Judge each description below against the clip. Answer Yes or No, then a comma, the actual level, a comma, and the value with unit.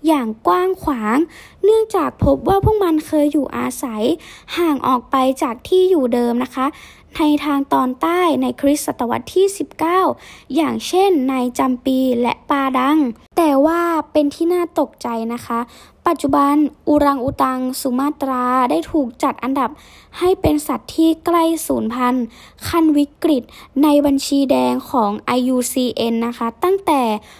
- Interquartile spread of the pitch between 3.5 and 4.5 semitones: Yes, average, 4.2 semitones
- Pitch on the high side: Yes, very high, 285 Hz